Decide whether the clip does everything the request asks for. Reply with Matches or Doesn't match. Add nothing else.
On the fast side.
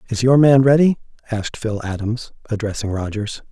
Doesn't match